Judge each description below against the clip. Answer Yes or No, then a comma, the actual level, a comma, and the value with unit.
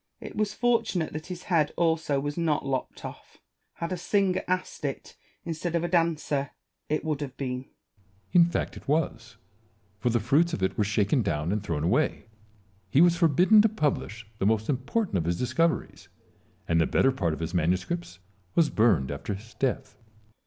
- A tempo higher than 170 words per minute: Yes, average, 190 wpm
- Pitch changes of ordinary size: No, wide, 8.0 semitones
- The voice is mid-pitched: Yes, medium, 145 Hz